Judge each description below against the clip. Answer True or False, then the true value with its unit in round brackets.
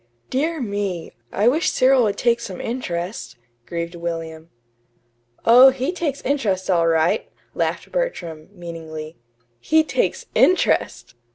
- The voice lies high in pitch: True (200 Hz)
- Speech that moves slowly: True (120 wpm)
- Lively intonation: True (8.0 semitones)